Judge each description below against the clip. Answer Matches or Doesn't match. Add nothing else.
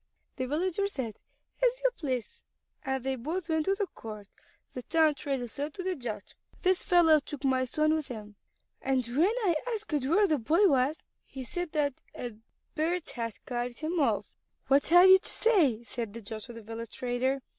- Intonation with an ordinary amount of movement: Doesn't match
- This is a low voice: Doesn't match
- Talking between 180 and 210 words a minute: Matches